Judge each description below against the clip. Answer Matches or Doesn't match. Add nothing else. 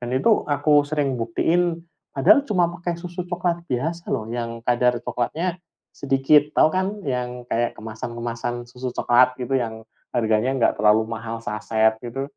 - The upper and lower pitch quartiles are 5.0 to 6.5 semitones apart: Matches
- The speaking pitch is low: Matches